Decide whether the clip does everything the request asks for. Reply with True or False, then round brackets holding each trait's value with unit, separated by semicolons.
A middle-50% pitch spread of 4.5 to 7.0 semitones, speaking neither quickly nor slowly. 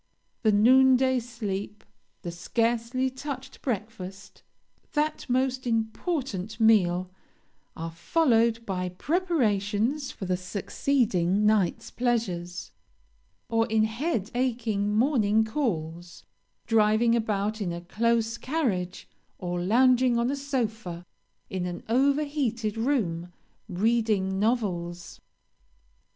False (4.9 semitones; 105 wpm)